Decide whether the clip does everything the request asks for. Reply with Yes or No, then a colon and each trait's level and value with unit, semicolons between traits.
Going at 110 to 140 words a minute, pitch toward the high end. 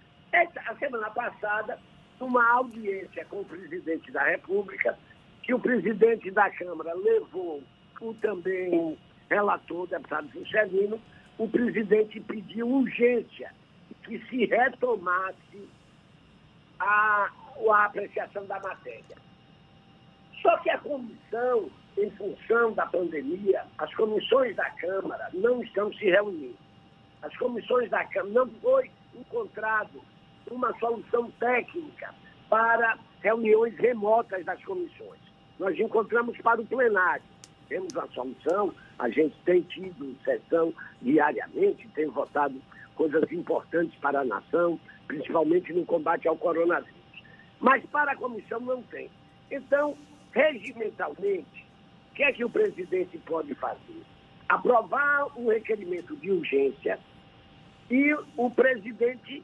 Yes: slow, 120 wpm; high, 235 Hz